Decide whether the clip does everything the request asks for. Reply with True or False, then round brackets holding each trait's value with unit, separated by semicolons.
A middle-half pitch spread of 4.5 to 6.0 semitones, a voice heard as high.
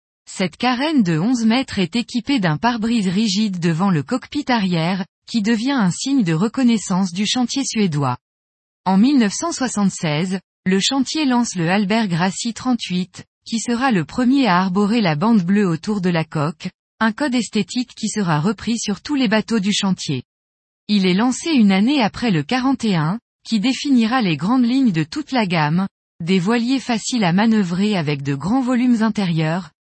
True (5.1 semitones; 210 Hz)